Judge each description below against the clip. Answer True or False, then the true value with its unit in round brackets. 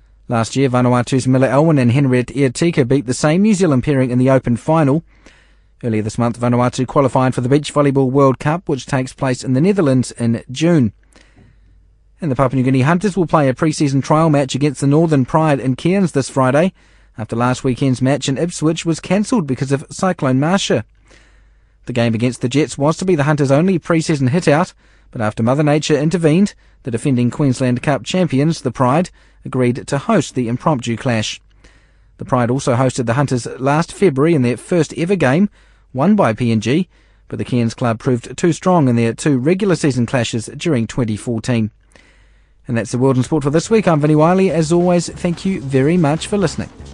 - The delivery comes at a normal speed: True (195 wpm)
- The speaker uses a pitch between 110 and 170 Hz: True (135 Hz)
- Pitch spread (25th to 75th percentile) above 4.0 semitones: True (4.5 semitones)